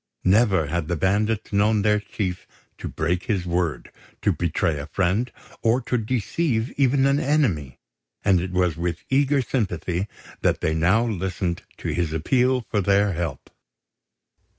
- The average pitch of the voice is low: Yes, low, 100 Hz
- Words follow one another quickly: No, average, 150 wpm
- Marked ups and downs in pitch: No, average, 5.0 semitones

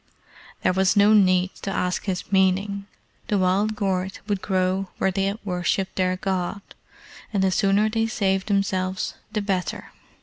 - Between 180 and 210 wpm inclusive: No, average, 160 wpm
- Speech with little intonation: Yes, narrow, 1.5 semitones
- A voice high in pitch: Yes, high, 195 Hz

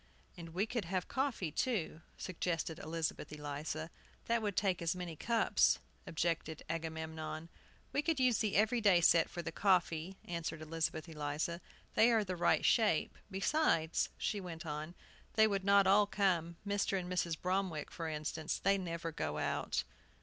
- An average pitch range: Yes, average, 3.8 semitones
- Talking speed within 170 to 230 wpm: No, average, 160 wpm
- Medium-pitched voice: Yes, medium, 175 Hz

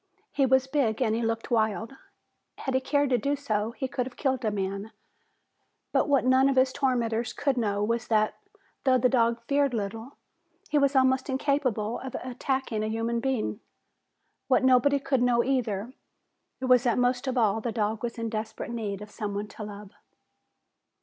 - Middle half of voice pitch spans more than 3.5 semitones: No, average, 3.2 semitones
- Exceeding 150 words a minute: Yes, average, 180 wpm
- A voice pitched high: Yes, high, 240 Hz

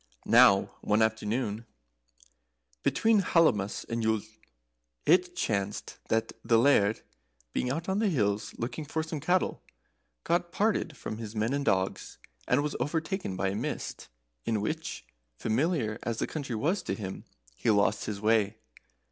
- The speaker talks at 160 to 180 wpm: No, average, 150 wpm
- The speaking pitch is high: No, low, 115 Hz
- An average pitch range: No, wide, 7.2 semitones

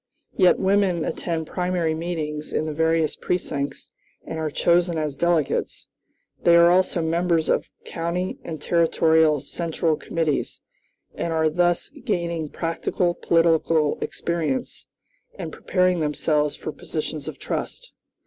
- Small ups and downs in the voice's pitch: Yes, narrow, 1.8 semitones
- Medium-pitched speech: Yes, medium, 165 Hz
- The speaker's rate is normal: No, slow, 125 wpm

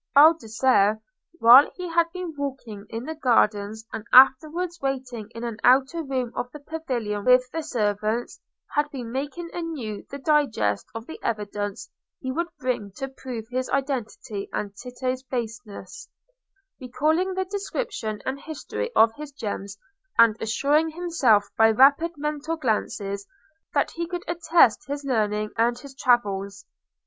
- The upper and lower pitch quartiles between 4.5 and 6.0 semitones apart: Yes, wide, 5.5 semitones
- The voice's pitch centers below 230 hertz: No, very high, 255 Hz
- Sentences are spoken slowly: No, average, 145 wpm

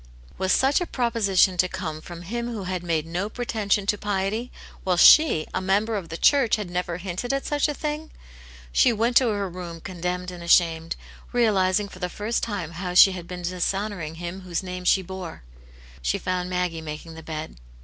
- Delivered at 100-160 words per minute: No, average, 195 wpm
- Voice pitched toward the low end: No, medium, 185 Hz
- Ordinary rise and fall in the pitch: Yes, average, 3.4 semitones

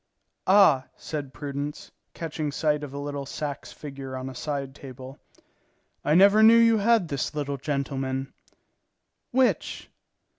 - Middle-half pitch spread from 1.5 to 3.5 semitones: Yes, average, 2.9 semitones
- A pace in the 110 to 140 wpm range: Yes, slow, 135 wpm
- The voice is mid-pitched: Yes, medium, 145 Hz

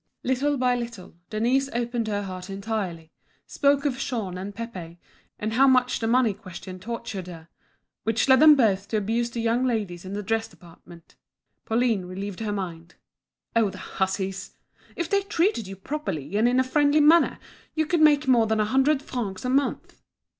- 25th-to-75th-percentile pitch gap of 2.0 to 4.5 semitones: No, average, 5.2 semitones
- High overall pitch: Yes, high, 225 Hz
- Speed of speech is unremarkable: Yes, average, 180 wpm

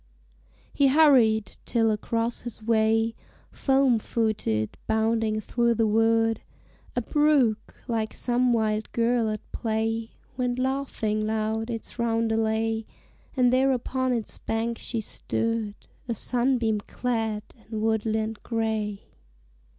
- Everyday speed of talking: No, slow, 115 wpm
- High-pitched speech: Yes, high, 225 Hz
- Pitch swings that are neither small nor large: No, narrow, 1.7 semitones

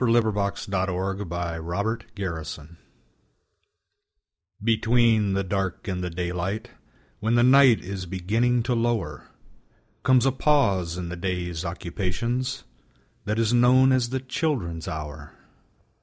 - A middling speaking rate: No, slow, 125 wpm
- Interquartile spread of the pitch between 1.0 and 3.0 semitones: No, average, 5.1 semitones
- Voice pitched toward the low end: Yes, low, 100 Hz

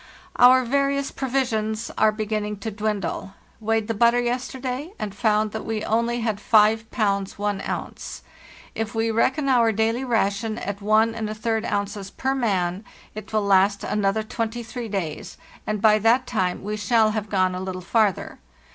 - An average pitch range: No, narrow, 2.3 semitones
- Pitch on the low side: No, high, 220 Hz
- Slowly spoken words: No, average, 155 wpm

